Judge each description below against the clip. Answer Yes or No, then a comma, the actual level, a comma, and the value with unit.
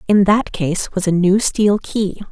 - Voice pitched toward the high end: Yes, high, 195 Hz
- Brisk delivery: Yes, fast, 210 wpm